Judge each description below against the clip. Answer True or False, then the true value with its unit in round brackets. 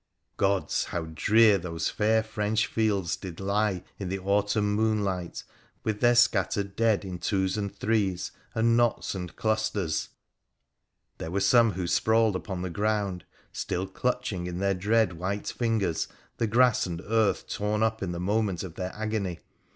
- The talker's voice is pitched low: True (100 Hz)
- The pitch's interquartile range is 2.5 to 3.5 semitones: True (3.0 semitones)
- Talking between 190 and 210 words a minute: False (160 wpm)